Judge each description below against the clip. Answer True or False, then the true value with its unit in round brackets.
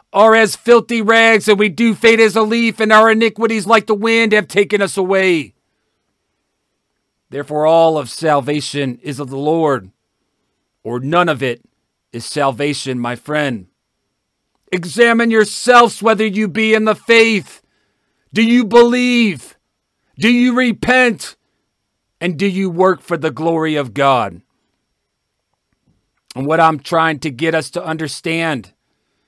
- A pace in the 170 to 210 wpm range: False (140 wpm)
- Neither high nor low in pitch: True (175 Hz)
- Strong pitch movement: True (7.6 semitones)